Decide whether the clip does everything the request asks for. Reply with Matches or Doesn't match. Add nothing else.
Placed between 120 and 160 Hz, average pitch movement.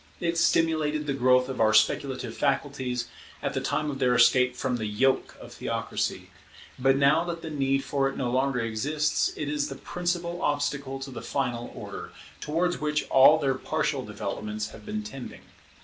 Matches